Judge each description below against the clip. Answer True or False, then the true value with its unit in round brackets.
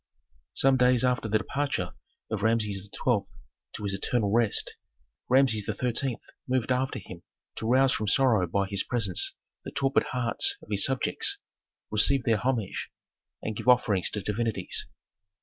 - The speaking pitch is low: True (115 Hz)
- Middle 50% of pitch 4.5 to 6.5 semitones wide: False (3.7 semitones)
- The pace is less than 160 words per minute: True (150 wpm)